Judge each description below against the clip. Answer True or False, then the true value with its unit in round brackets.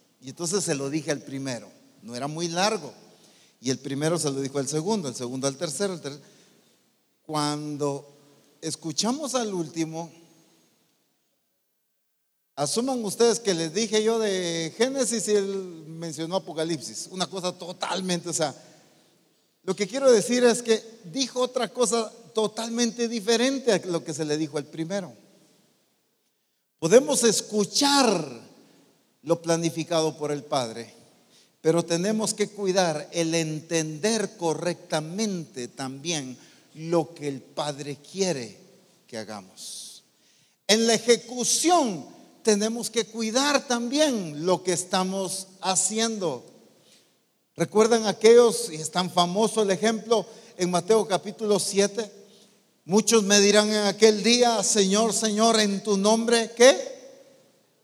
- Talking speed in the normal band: False (125 wpm)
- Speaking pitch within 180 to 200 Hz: True (190 Hz)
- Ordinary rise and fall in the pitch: False (5.7 semitones)